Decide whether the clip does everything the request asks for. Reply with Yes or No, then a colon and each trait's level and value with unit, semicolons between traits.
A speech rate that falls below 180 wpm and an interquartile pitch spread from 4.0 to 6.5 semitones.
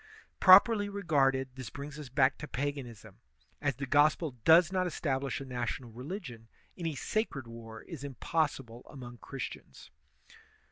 Yes: slow, 135 wpm; average, 4.3 semitones